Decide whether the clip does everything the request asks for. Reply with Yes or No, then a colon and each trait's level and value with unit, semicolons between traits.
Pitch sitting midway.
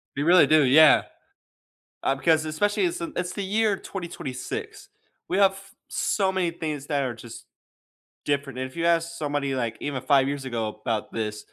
Yes: medium, 150 Hz